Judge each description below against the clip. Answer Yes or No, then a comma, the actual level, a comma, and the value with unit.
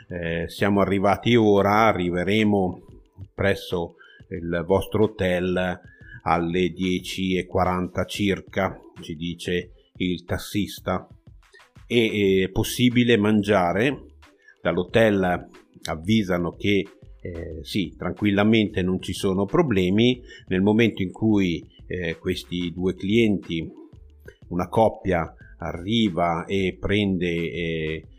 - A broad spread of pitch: No, average, 3.1 semitones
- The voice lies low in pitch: Yes, very low, 95 Hz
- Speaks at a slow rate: Yes, slow, 95 wpm